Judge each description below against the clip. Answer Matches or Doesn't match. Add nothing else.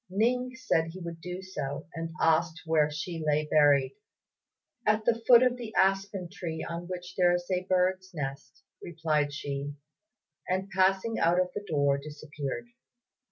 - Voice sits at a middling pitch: Matches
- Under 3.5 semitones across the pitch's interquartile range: Doesn't match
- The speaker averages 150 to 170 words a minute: Matches